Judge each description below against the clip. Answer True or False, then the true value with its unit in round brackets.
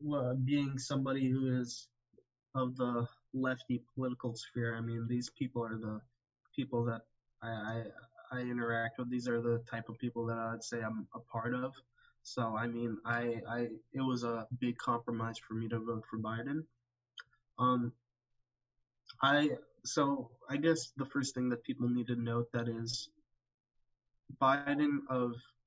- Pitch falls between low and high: False (120 Hz)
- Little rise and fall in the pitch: True (1.7 semitones)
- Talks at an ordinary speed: True (165 wpm)